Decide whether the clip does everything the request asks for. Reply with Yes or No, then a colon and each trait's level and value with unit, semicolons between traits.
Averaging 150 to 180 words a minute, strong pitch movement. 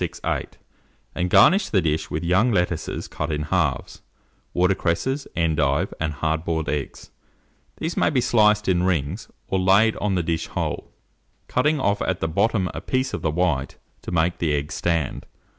No: average, 175 wpm; average, 4.3 semitones